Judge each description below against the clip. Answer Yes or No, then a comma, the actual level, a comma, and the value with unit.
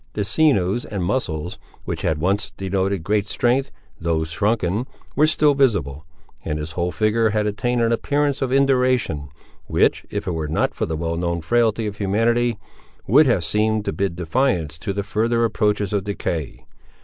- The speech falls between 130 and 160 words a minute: No, average, 175 wpm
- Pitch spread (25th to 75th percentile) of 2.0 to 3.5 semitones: No, wide, 5.6 semitones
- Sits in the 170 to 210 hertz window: No, low, 105 Hz